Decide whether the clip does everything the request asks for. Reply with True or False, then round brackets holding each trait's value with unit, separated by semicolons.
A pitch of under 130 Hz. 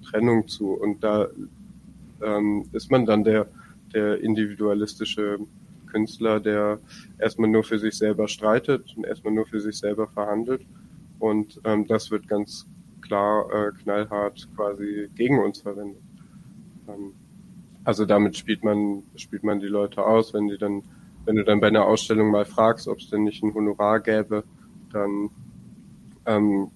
True (105 Hz)